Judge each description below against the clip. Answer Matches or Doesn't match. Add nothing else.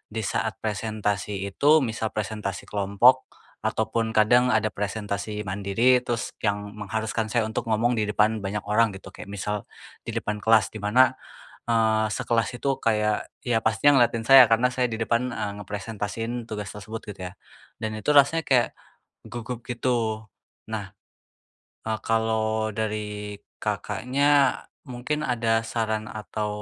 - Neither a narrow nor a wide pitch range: Doesn't match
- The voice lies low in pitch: Matches